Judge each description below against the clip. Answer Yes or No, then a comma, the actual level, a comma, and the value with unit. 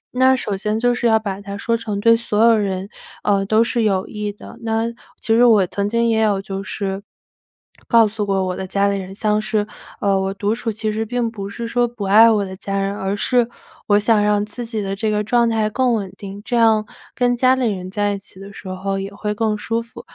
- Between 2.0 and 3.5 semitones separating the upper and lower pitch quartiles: Yes, narrow, 2.5 semitones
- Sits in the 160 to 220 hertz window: Yes, high, 210 Hz